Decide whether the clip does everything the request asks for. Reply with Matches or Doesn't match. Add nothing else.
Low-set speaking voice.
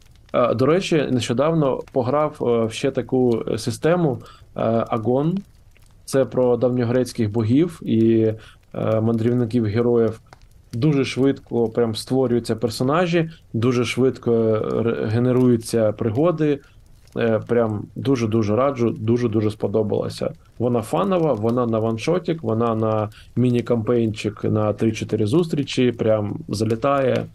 Matches